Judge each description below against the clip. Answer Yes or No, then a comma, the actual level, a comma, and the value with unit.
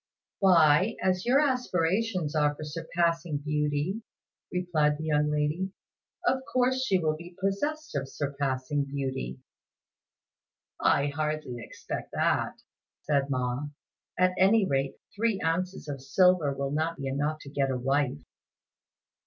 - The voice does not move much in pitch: No, average, 4.5 semitones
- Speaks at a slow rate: Yes, slow, 130 wpm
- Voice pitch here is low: No, medium, 155 Hz